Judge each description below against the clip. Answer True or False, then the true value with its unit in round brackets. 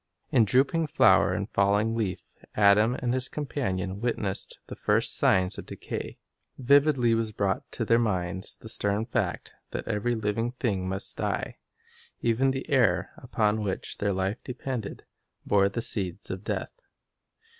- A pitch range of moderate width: True (3.8 semitones)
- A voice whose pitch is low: True (110 Hz)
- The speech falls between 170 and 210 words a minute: False (150 wpm)